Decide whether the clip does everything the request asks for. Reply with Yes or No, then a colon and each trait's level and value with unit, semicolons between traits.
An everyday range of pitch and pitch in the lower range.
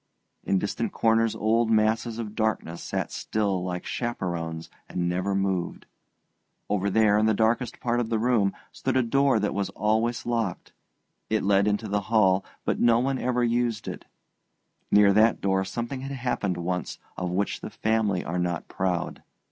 Yes: average, 3.5 semitones; low, 110 Hz